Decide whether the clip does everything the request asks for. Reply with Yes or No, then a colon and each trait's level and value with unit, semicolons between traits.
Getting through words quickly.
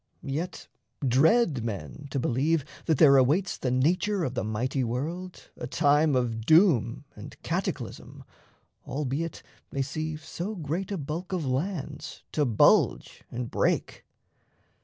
No: slow, 135 wpm